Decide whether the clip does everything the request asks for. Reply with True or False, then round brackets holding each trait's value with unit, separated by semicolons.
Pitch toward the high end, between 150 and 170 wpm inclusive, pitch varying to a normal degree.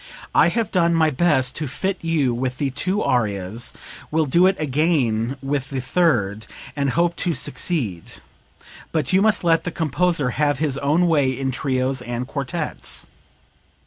False (145 Hz; 160 wpm; 4.7 semitones)